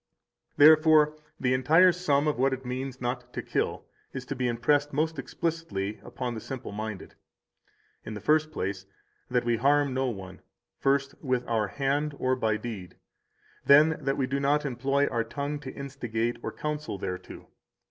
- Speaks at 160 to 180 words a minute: Yes, average, 170 wpm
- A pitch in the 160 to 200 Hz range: No, low, 130 Hz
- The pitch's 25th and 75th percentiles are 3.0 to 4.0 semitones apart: Yes, average, 3.6 semitones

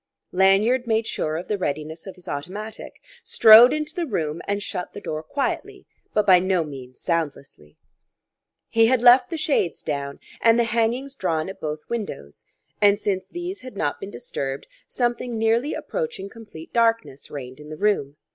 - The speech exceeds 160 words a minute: Yes, average, 170 wpm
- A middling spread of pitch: No, wide, 7.1 semitones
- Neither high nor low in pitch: No, high, 200 Hz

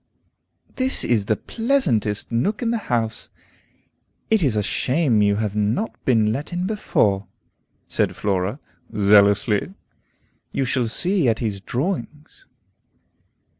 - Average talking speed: No, slow, 120 wpm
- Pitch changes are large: Yes, wide, 8.9 semitones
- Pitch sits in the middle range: No, low, 115 Hz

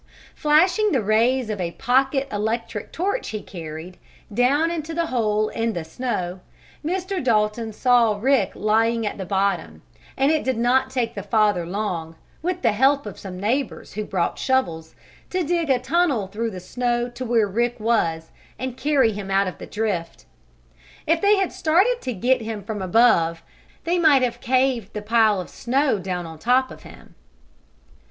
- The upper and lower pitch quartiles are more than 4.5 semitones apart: Yes, average, 5.0 semitones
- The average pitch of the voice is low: No, high, 230 Hz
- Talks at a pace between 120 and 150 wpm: No, average, 175 wpm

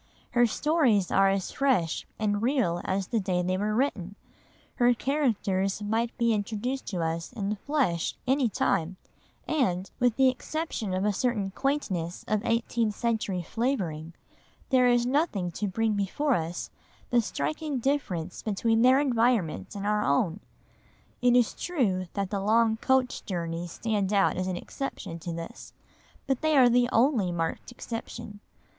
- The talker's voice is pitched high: Yes, high, 215 Hz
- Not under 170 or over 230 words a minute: No, average, 155 wpm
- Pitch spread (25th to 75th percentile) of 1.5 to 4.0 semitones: No, average, 5.0 semitones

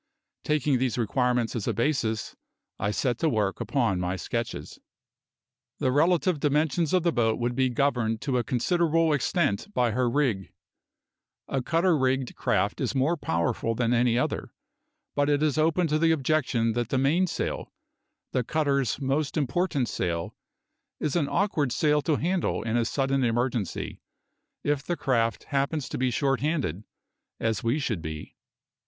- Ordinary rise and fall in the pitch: Yes, average, 4.5 semitones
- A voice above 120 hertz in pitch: Yes, low, 135 Hz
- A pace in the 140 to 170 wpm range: Yes, average, 160 wpm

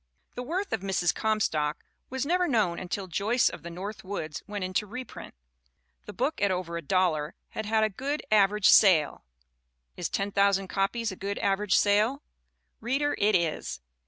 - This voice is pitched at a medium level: No, high, 200 Hz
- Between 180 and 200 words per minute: No, average, 170 wpm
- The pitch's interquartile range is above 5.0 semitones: No, average, 3.3 semitones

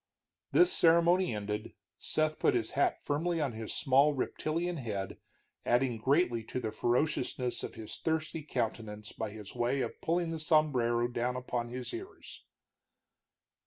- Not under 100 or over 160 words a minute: Yes, average, 145 wpm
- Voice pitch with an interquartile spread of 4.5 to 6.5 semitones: Yes, average, 5.2 semitones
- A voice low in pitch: Yes, low, 130 Hz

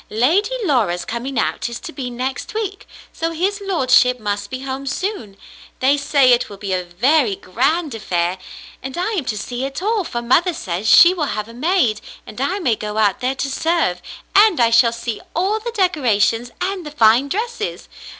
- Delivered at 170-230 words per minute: Yes, average, 195 wpm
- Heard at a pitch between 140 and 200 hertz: No, very high, 260 Hz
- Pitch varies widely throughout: Yes, wide, 7.8 semitones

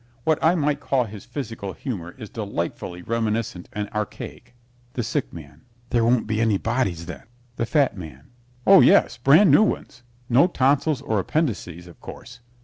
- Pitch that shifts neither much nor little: No, wide, 5.7 semitones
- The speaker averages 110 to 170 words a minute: Yes, average, 165 wpm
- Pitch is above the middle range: No, low, 115 Hz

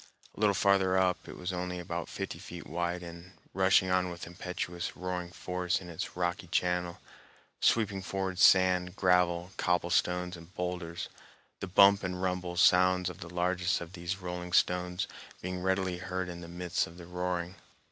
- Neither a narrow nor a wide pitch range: No, narrow, 0.9 semitones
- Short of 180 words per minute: Yes, average, 165 wpm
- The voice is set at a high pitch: No, very low, 90 Hz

